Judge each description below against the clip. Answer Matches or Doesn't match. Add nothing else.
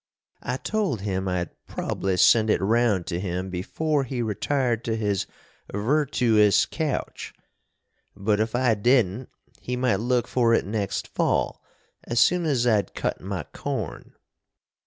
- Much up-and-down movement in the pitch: Doesn't match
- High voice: Doesn't match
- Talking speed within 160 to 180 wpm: Doesn't match